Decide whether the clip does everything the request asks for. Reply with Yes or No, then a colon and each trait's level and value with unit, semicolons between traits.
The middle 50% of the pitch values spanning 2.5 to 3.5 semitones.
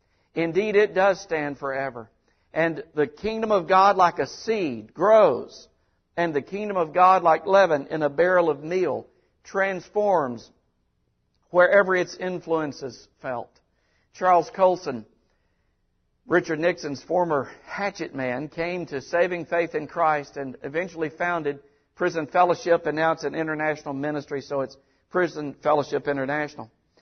No: average, 4.1 semitones